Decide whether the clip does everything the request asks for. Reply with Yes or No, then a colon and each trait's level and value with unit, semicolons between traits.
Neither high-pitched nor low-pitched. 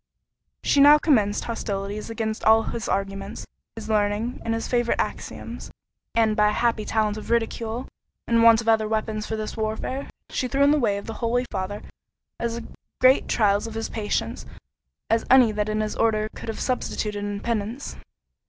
No: high, 220 Hz